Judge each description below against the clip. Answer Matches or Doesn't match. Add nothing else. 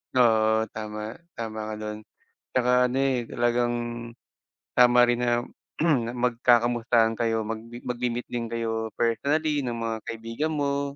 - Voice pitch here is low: Matches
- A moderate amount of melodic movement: Doesn't match